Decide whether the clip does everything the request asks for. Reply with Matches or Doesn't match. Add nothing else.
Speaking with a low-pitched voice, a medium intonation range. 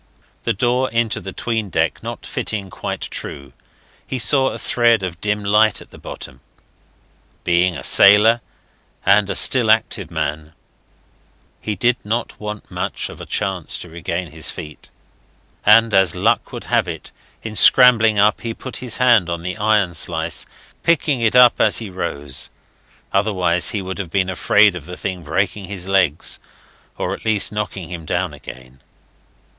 Matches